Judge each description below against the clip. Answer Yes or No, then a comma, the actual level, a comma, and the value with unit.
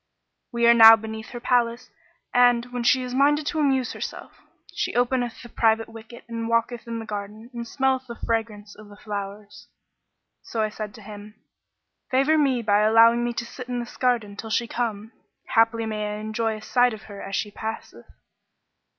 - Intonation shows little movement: Yes, narrow, 2.2 semitones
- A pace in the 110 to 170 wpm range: No, average, 190 wpm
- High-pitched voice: Yes, high, 230 Hz